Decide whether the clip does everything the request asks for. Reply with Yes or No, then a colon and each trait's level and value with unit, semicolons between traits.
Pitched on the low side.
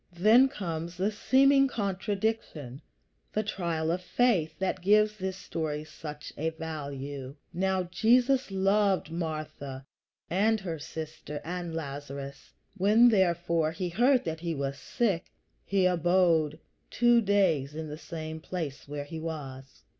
No: medium, 170 Hz